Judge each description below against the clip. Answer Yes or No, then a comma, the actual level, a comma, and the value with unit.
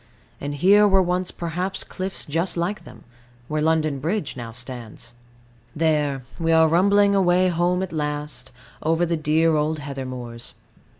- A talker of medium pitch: Yes, medium, 160 Hz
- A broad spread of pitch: No, average, 3.8 semitones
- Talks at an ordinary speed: Yes, average, 155 wpm